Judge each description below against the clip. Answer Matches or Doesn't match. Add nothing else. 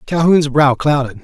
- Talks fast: Doesn't match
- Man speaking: Matches